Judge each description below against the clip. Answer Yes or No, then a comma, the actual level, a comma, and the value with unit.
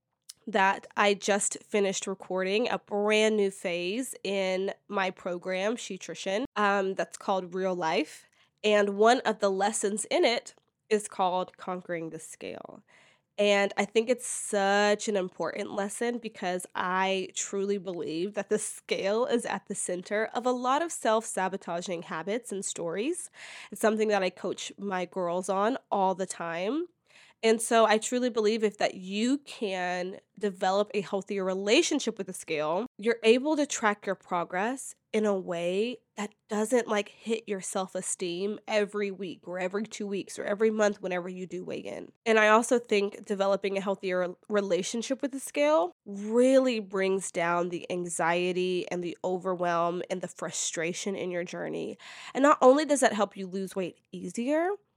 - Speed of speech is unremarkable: Yes, average, 165 wpm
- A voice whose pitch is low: No, high, 200 Hz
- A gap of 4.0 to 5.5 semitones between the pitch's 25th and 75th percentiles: No, average, 3.1 semitones